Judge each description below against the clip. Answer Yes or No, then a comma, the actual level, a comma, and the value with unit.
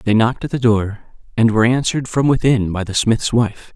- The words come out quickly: Yes, fast, 225 wpm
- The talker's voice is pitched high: No, low, 115 Hz